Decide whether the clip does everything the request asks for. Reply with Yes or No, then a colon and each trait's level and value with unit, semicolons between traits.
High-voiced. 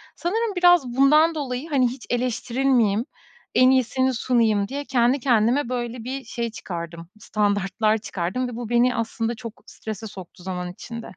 Yes: high, 240 Hz